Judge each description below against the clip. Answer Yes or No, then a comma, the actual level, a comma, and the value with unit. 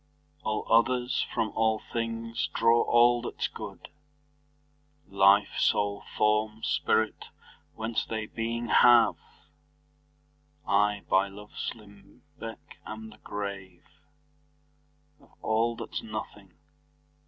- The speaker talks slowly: Yes, slow, 95 wpm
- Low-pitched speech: Yes, low, 110 Hz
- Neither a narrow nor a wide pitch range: No, narrow, 2.0 semitones